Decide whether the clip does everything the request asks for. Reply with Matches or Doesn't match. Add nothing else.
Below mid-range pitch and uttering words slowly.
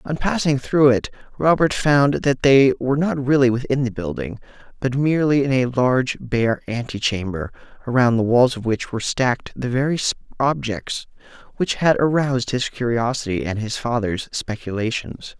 Doesn't match